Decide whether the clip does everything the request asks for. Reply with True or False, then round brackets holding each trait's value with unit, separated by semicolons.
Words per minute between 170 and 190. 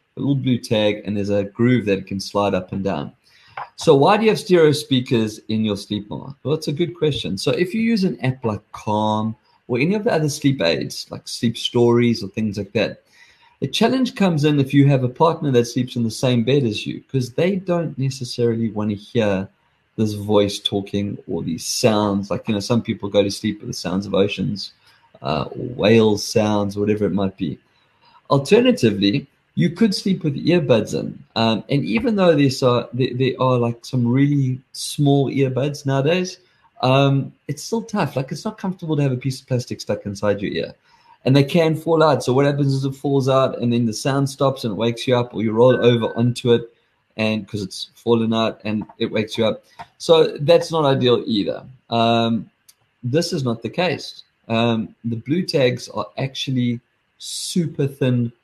False (200 wpm)